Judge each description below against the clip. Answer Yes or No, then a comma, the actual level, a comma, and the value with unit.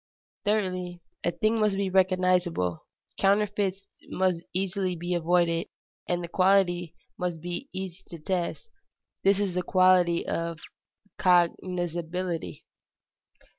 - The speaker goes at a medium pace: No, slow, 110 wpm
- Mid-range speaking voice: Yes, medium, 180 Hz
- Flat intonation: Yes, narrow, 1.8 semitones